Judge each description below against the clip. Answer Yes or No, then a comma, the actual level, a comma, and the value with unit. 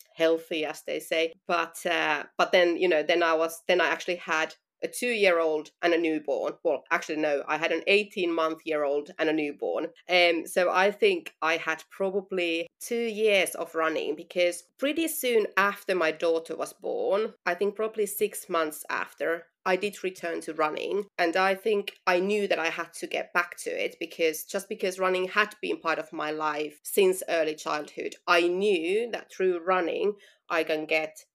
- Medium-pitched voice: Yes, medium, 175 Hz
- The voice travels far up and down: No, average, 4.0 semitones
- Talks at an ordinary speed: Yes, average, 190 wpm